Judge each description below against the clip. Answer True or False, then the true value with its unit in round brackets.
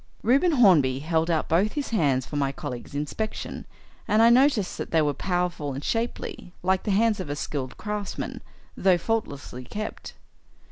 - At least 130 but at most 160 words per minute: False (170 wpm)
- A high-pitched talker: False (180 Hz)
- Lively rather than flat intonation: True (6.9 semitones)